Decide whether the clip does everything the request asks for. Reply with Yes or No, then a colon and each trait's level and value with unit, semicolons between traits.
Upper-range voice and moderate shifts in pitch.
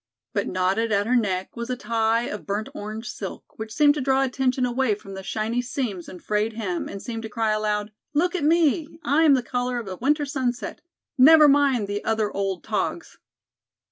Yes: high, 230 Hz; average, 4.1 semitones